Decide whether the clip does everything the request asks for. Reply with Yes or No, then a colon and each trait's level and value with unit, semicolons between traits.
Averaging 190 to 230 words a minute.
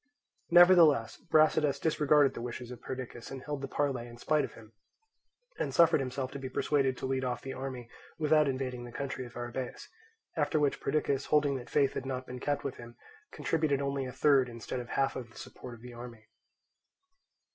Yes: average, 195 wpm